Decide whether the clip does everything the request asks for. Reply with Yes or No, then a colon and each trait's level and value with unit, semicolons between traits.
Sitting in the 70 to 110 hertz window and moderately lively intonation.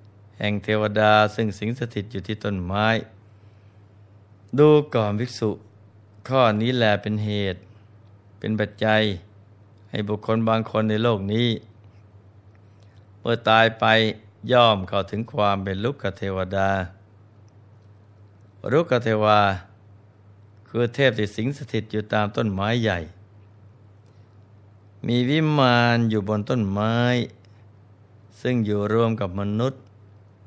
No: low, 105 Hz; narrow, 1.5 semitones